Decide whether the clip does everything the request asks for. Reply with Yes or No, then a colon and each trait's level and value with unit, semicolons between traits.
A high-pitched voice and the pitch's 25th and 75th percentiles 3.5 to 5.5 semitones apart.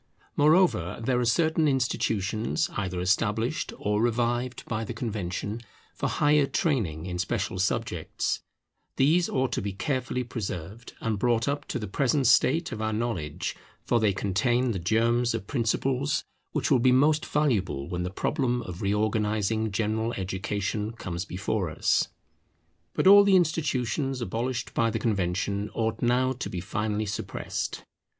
No: low, 115 Hz; average, 4.4 semitones